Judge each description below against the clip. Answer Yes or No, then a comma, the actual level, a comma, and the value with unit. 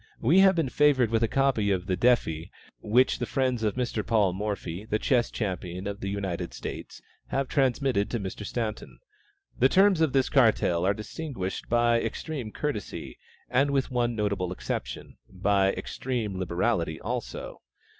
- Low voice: Yes, low, 115 Hz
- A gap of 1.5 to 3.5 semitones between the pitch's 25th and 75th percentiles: No, average, 4.9 semitones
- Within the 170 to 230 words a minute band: No, average, 160 wpm